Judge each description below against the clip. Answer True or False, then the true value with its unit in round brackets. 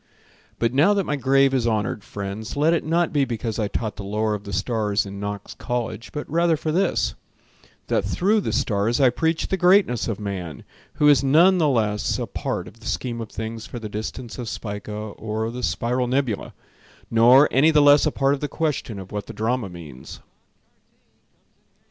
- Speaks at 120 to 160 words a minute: False (195 wpm)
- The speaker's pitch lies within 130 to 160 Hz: False (120 Hz)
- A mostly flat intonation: False (5.5 semitones)